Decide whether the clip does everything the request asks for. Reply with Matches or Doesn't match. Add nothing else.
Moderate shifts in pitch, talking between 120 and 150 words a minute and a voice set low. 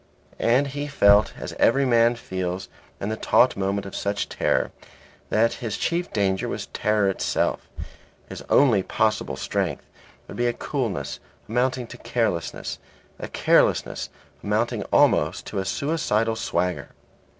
Matches